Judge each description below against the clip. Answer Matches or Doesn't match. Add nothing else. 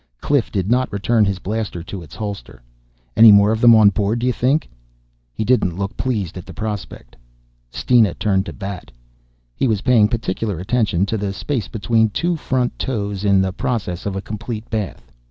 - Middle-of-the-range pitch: Doesn't match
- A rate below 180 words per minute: Doesn't match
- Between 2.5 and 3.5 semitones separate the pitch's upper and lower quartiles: Matches